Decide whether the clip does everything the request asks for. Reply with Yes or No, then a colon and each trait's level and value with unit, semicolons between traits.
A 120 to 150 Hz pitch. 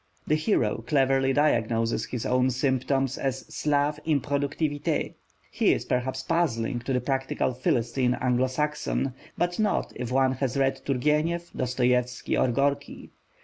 Yes: low, 135 Hz